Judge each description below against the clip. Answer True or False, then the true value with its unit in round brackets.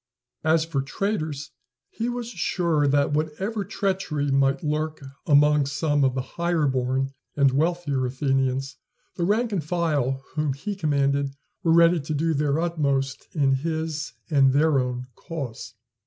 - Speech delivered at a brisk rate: False (145 wpm)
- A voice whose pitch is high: False (150 Hz)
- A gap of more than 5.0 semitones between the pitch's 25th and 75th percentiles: False (3.4 semitones)